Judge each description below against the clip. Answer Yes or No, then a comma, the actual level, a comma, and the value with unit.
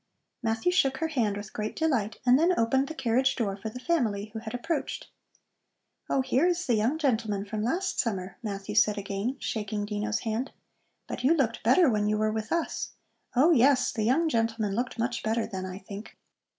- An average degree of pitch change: Yes, average, 4.0 semitones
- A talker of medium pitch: No, high, 230 Hz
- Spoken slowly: No, average, 195 wpm